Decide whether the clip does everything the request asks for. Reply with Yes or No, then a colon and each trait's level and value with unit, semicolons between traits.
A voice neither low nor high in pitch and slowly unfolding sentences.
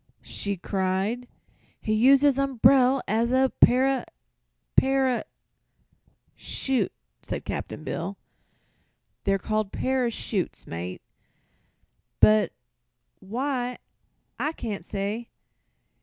No: high, 240 Hz; slow, 90 wpm